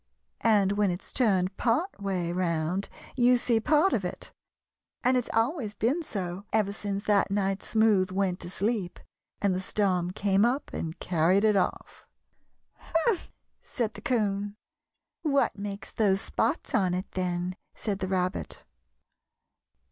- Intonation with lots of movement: No, average, 3.3 semitones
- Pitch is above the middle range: Yes, high, 200 Hz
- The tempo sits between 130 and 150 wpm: Yes, average, 145 wpm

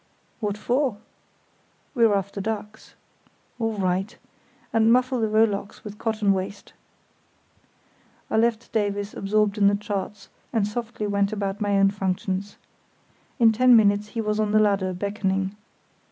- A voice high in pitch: Yes, high, 210 Hz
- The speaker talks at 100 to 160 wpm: Yes, average, 140 wpm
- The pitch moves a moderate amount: No, narrow, 1.8 semitones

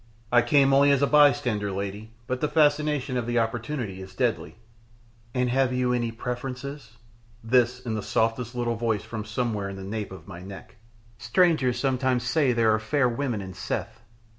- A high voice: No, low, 120 Hz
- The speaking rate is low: No, average, 185 wpm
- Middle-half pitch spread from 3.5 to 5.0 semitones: No, average, 3.1 semitones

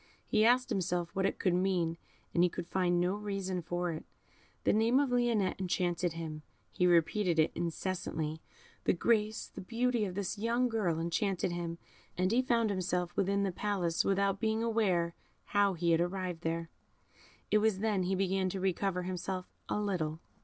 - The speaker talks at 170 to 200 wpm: Yes, average, 175 wpm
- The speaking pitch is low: No, medium, 185 Hz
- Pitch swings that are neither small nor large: Yes, average, 3.2 semitones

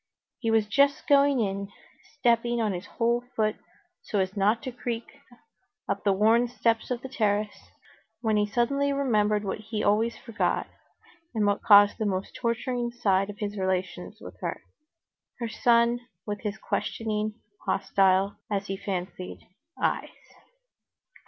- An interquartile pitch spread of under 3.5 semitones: Yes, average, 2.8 semitones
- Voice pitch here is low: No, high, 215 Hz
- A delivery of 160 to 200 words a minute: No, average, 140 wpm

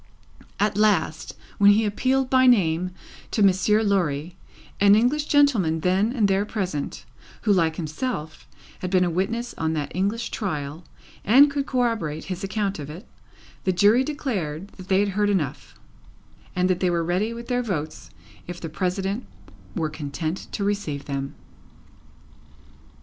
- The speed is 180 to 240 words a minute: No, average, 155 wpm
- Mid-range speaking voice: No, high, 195 Hz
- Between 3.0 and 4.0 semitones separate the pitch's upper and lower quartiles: No, average, 5.1 semitones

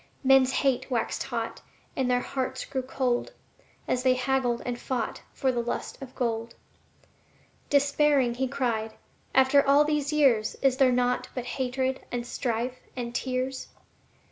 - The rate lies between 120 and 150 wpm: Yes, average, 145 wpm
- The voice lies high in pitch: Yes, very high, 255 Hz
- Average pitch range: No, narrow, 1.6 semitones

